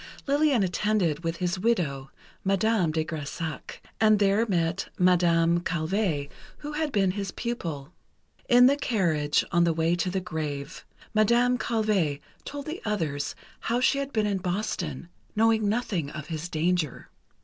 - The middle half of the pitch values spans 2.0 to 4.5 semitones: No, average, 5.2 semitones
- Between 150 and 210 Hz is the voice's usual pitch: Yes, medium, 185 Hz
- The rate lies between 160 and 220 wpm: No, average, 150 wpm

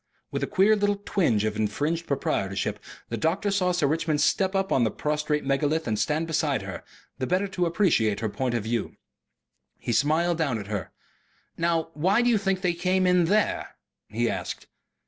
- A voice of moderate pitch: Yes, medium, 160 Hz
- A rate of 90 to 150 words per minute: No, average, 185 wpm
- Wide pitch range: Yes, wide, 7.7 semitones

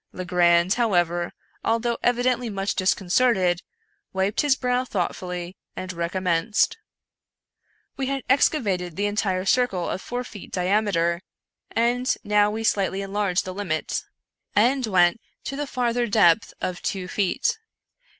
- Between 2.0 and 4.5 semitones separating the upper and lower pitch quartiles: No, average, 4.9 semitones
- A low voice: No, high, 200 Hz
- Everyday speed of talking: No, slow, 125 wpm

